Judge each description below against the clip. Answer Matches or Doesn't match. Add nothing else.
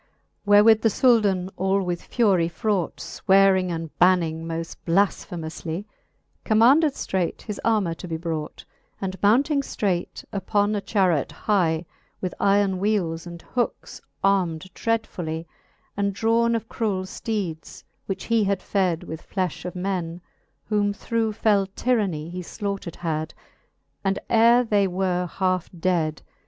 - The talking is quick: Doesn't match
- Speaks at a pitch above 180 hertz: Matches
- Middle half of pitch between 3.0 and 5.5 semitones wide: Matches